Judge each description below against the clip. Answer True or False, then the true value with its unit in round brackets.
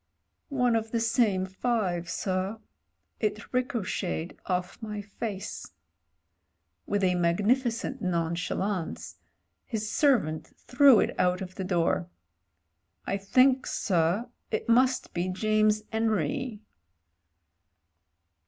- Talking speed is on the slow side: True (100 wpm)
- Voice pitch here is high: True (205 Hz)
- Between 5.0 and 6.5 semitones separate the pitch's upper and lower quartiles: False (4.1 semitones)